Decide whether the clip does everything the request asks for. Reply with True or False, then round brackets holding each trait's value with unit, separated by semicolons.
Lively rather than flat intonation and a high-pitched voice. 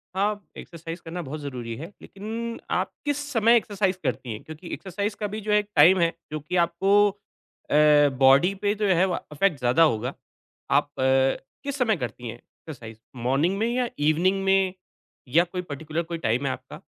False (6.1 semitones; 175 Hz)